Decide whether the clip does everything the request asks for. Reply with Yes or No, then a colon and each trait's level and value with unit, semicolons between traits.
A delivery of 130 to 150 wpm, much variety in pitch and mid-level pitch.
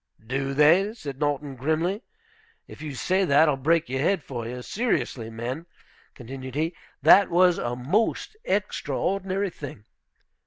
Yes: average, 145 wpm; wide, 5.8 semitones; medium, 150 Hz